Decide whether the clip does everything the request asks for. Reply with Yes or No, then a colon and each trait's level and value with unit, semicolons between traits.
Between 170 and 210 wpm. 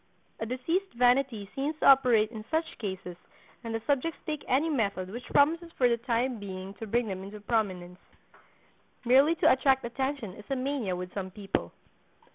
Yes: average, 175 wpm